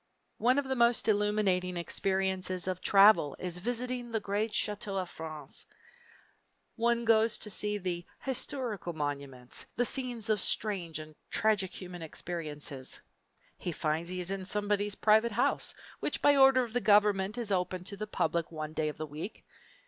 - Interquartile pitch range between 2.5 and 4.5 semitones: Yes, average, 4.2 semitones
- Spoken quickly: No, average, 160 wpm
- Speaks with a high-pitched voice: Yes, high, 195 Hz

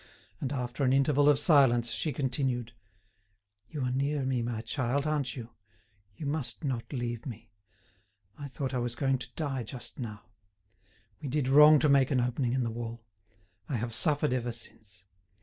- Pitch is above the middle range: No, low, 130 Hz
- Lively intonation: No, average, 3.0 semitones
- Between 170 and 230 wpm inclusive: Yes, average, 175 wpm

